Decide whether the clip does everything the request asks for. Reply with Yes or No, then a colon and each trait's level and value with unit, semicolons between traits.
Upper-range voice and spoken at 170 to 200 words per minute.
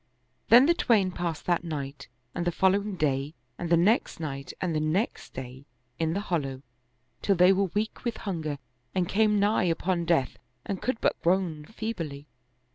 No: medium, 175 Hz; average, 175 wpm